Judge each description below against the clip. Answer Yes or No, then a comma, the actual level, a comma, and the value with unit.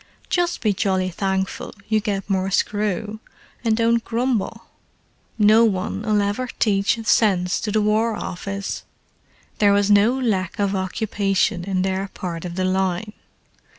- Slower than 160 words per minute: Yes, average, 140 wpm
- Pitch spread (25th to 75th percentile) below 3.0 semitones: Yes, narrow, 2.4 semitones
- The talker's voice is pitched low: No, high, 205 Hz